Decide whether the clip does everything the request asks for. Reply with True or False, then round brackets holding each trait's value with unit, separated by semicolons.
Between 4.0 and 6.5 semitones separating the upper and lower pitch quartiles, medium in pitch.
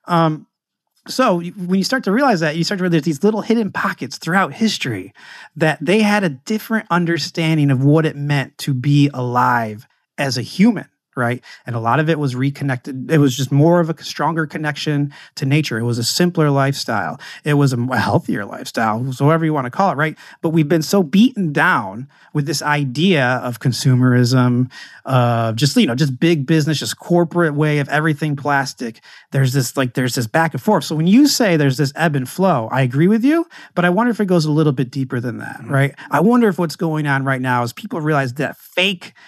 True (4.5 semitones; 150 Hz)